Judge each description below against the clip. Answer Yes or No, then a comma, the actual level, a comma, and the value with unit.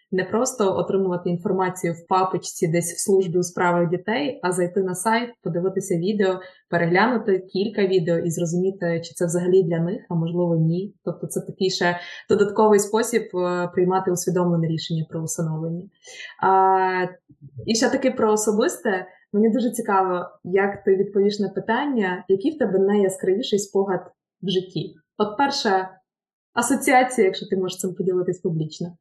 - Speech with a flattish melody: Yes, narrow, 2.3 semitones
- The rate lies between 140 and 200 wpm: Yes, average, 150 wpm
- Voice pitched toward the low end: No, high, 190 Hz